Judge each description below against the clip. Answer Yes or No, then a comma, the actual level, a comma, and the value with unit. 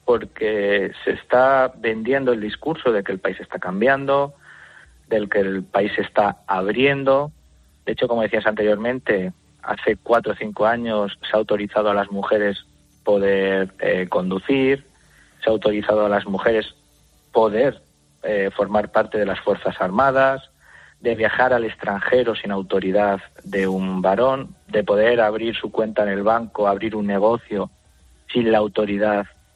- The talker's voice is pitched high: No, low, 105 Hz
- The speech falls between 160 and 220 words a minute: No, average, 150 wpm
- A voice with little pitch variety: No, average, 3.4 semitones